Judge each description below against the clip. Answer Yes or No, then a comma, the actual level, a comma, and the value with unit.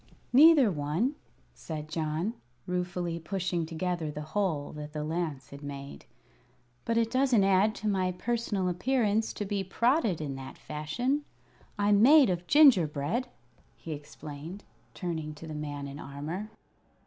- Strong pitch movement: Yes, wide, 5.8 semitones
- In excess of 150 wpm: No, average, 140 wpm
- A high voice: No, medium, 175 Hz